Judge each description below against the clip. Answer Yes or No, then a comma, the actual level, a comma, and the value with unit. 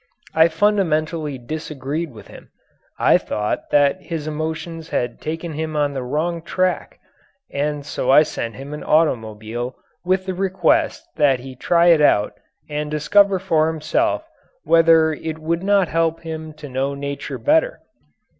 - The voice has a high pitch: No, medium, 155 Hz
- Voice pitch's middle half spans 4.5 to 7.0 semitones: No, average, 2.9 semitones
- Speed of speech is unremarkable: Yes, average, 150 wpm